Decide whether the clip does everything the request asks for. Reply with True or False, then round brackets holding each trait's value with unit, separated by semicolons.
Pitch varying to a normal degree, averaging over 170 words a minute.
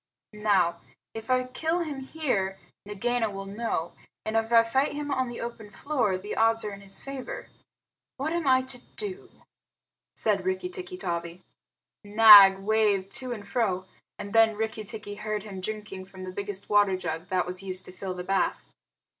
True (4.0 semitones; 180 wpm)